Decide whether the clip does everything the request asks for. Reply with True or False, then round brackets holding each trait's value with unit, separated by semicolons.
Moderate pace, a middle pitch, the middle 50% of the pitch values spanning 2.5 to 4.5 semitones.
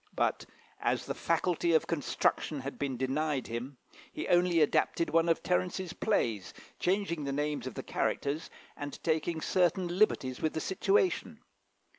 True (150 wpm; 160 Hz; 4.1 semitones)